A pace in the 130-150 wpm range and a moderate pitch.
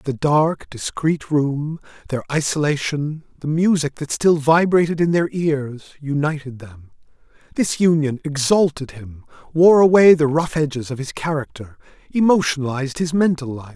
Yes: average, 140 wpm; medium, 150 Hz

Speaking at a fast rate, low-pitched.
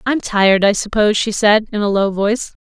No: fast, 230 wpm; high, 210 Hz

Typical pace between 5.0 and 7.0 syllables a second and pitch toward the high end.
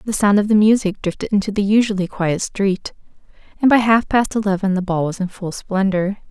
Yes: 5.6 syllables/s; high, 200 Hz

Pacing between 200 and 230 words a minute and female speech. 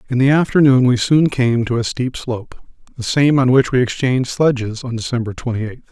No: fast, 205 wpm; male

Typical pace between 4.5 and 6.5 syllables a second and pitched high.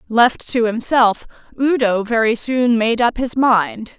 No: 3.7 syllables/s; high, 235 Hz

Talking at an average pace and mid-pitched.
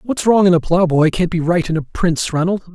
No: fast, 265 wpm; medium, 175 Hz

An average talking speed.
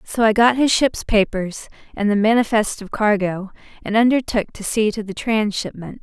Yes: average, 190 wpm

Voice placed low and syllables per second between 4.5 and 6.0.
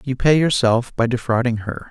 Yes: low, 125 Hz; 5.0 syllables/s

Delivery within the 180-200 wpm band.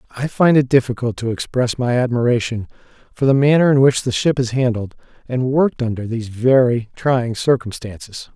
No: average, 170 wpm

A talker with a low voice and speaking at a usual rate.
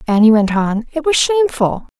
No: very high, 255 Hz; average, 180 wpm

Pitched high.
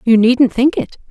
Yes: high, 245 Hz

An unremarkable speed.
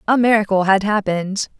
Yes: average, 150 wpm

